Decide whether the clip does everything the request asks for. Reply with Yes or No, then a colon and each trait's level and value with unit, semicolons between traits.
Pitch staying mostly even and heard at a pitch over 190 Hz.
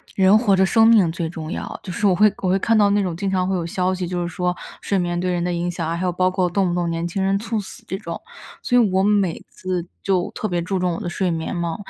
No: narrow, 2.1 semitones; medium, 185 Hz